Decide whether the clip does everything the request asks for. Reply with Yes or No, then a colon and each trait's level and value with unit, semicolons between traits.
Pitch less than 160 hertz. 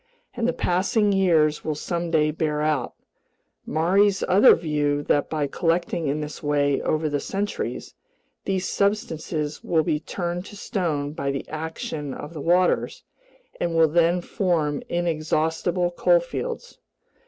No: medium, 165 Hz